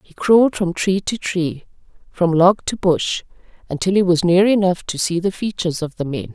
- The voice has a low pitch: No, medium, 180 Hz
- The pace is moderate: No, fast, 210 wpm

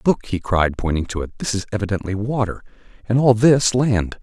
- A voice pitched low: Yes, low, 105 Hz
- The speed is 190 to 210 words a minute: Yes, average, 200 wpm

